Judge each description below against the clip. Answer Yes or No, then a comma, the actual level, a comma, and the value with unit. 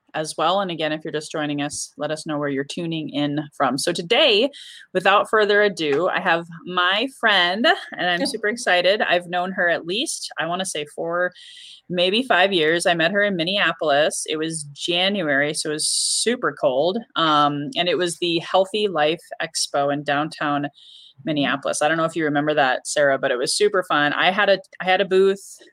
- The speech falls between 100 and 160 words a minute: No, fast, 205 wpm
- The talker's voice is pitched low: No, medium, 170 Hz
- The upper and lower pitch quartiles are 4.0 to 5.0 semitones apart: Yes, average, 4.4 semitones